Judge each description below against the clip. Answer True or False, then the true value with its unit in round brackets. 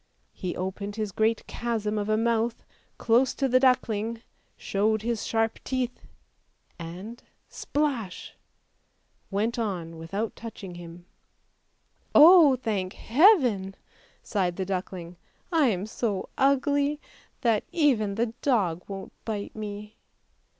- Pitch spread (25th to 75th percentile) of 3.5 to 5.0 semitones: True (3.8 semitones)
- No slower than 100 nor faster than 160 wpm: True (135 wpm)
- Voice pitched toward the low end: False (220 Hz)